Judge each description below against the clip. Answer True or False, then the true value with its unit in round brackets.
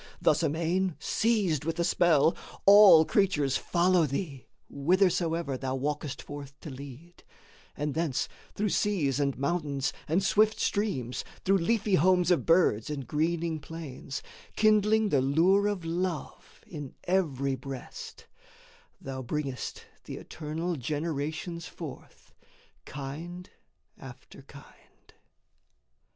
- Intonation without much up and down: False (4.6 semitones)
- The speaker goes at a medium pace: False (115 wpm)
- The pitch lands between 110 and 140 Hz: False (160 Hz)